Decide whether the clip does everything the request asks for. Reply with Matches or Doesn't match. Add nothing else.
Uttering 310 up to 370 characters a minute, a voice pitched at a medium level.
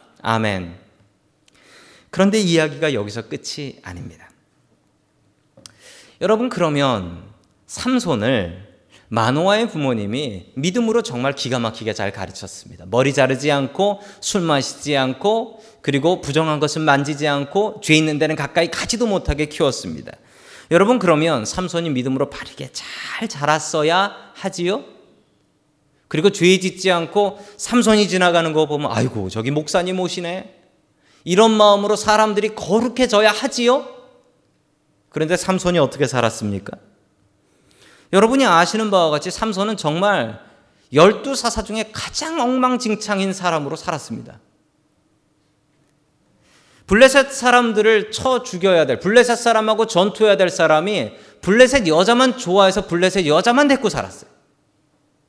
Doesn't match